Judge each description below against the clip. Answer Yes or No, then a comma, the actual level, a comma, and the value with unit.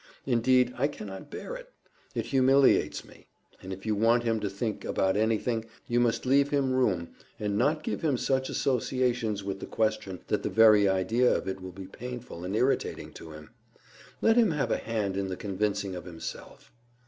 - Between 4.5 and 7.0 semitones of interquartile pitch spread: Yes, average, 4.9 semitones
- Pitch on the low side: Yes, low, 115 Hz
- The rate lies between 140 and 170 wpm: No, average, 190 wpm